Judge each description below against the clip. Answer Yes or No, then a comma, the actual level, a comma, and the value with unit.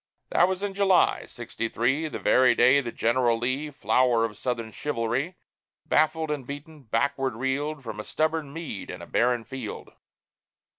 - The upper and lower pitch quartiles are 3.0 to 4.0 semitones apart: No, average, 4.5 semitones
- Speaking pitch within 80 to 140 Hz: Yes, low, 135 Hz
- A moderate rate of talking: Yes, average, 160 wpm